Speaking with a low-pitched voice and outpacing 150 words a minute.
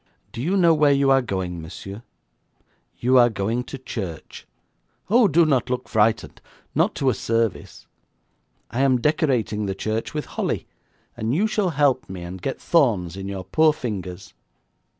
Yes: low, 120 Hz; average, 165 wpm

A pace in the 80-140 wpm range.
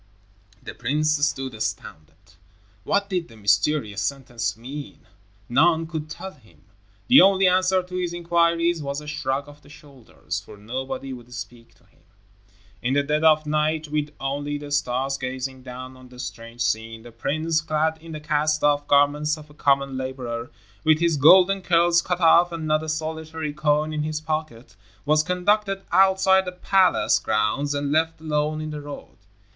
No: average, 175 wpm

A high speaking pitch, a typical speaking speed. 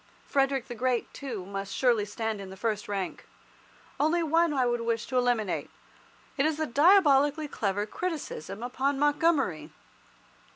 Yes: very high, 250 Hz; average, 150 wpm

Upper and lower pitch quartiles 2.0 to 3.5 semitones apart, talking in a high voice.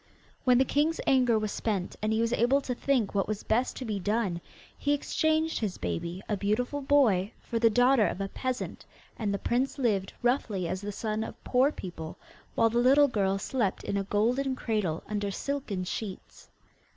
No: average, 4.4 semitones; high, 225 Hz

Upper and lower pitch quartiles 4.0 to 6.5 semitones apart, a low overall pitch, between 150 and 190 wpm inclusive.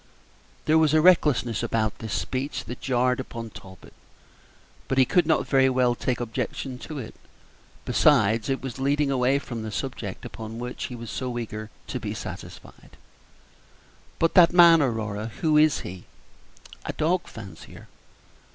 Yes: average, 4.4 semitones; low, 125 Hz; average, 155 wpm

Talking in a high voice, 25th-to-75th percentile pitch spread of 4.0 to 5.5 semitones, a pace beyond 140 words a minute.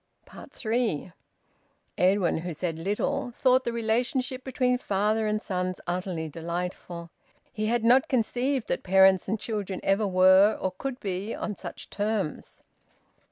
No: high, 205 Hz; average, 4.3 semitones; slow, 135 wpm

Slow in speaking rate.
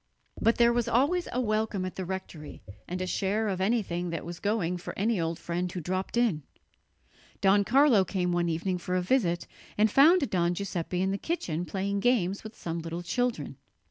No: average, 195 wpm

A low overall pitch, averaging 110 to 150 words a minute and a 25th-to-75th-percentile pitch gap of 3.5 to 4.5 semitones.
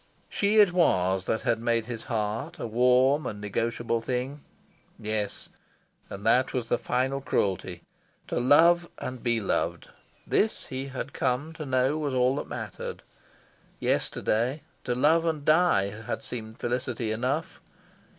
Yes: low, 125 Hz; average, 145 wpm; average, 4.1 semitones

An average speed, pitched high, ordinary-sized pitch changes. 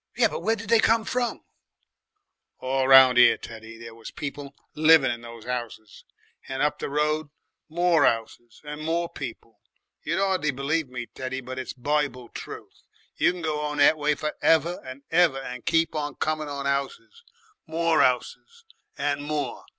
No: average, 170 wpm; medium, 145 Hz; average, 4.0 semitones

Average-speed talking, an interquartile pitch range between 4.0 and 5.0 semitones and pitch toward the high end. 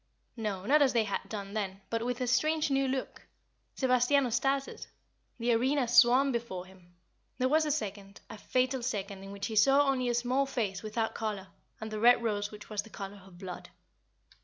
Yes: average, 195 wpm; average, 4.3 semitones; high, 235 Hz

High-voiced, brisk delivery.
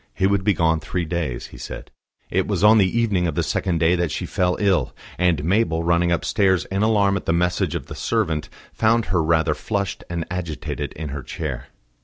No: very low, 85 Hz; fast, 210 wpm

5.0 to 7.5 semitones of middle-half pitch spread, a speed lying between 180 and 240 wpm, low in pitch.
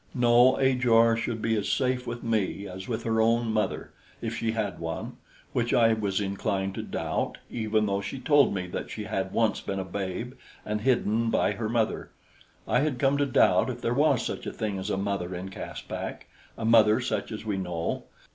No: average, 3.2 semitones; fast, 205 wpm; low, 110 Hz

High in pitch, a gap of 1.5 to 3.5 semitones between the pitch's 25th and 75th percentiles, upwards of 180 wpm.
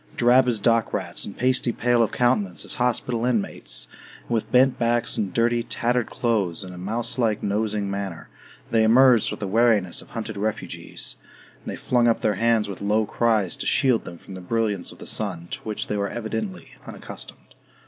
No: low, 110 Hz; average, 3.0 semitones; average, 195 wpm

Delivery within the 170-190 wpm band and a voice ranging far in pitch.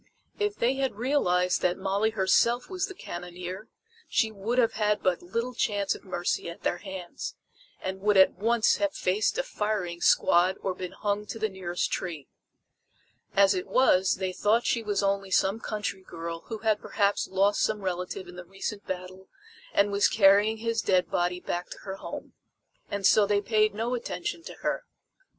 No: average, 180 wpm; average, 3.0 semitones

